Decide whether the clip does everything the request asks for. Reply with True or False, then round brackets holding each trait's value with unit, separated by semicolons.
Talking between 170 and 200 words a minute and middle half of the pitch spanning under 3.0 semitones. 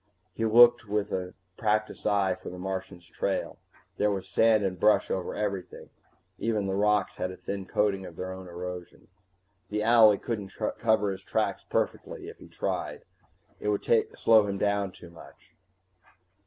False (160 wpm; 2.4 semitones)